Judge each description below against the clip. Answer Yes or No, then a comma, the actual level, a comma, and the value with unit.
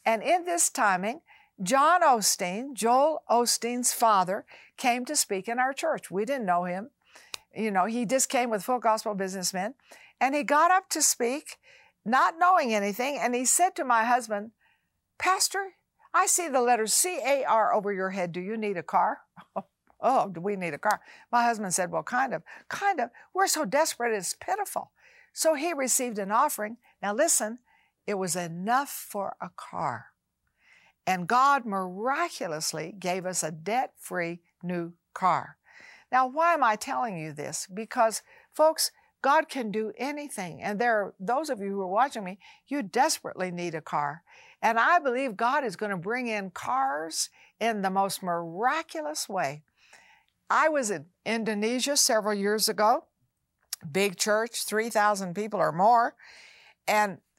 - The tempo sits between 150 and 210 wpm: Yes, average, 165 wpm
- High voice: Yes, high, 230 Hz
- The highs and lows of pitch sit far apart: Yes, wide, 6.2 semitones